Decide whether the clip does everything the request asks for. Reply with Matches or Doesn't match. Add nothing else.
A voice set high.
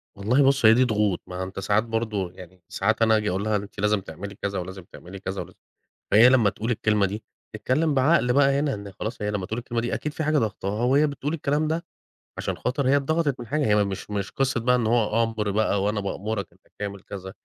Doesn't match